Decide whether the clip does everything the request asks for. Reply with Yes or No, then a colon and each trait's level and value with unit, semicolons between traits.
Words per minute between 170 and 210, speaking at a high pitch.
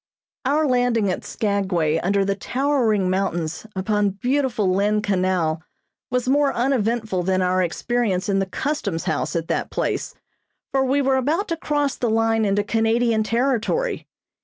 No: average, 150 wpm; high, 220 Hz